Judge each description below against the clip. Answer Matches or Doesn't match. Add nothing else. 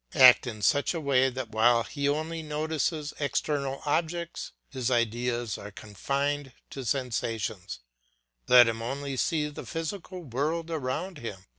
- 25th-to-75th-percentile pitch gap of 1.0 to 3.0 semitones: Doesn't match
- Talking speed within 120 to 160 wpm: Matches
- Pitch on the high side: Doesn't match